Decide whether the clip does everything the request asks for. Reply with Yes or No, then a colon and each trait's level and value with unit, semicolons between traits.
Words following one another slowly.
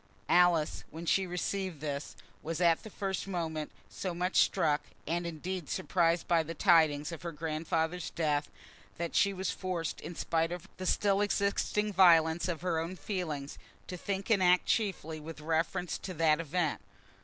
No: average, 165 wpm